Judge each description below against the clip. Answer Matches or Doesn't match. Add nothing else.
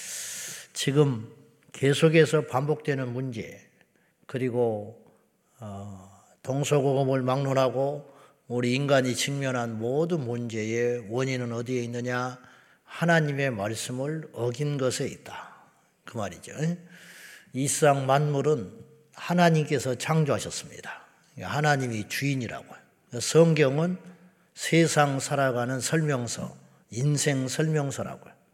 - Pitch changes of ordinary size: Matches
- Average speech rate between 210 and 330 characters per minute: Matches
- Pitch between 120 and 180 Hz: Matches